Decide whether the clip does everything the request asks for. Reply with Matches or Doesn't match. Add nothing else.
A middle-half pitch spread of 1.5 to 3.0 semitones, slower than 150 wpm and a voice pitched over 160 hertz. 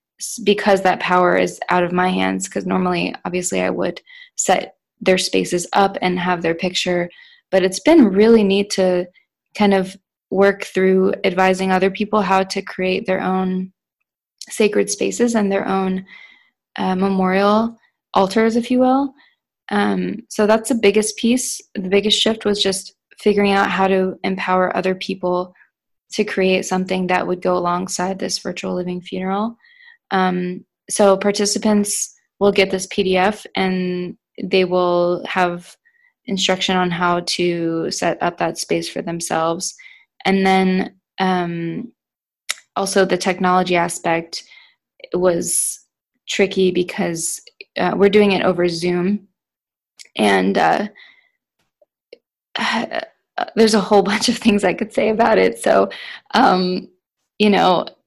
Matches